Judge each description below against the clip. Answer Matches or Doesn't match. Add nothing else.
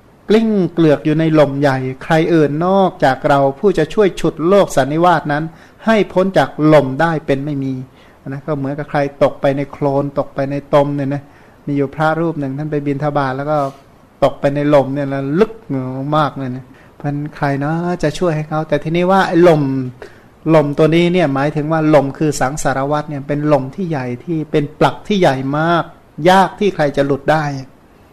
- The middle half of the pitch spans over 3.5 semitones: Doesn't match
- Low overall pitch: Doesn't match